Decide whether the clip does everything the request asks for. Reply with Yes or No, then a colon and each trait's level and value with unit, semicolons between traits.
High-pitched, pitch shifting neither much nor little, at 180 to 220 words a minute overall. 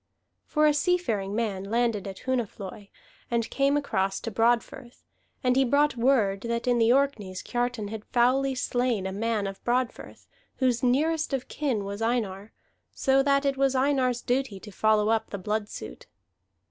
No: high, 240 Hz; average, 4.3 semitones; average, 165 wpm